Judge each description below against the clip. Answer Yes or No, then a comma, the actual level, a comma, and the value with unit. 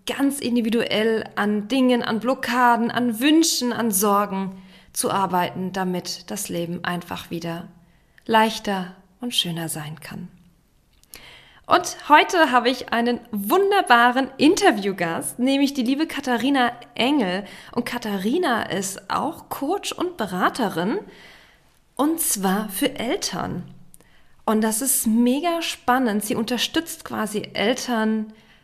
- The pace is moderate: No, slow, 115 wpm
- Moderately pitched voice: No, high, 235 Hz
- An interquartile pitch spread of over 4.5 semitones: Yes, average, 5.1 semitones